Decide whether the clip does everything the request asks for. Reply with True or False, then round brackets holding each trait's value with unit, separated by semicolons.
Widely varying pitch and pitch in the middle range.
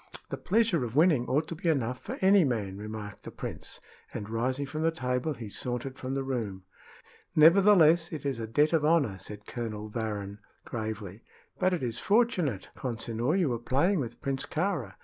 False (6.2 semitones; 130 Hz)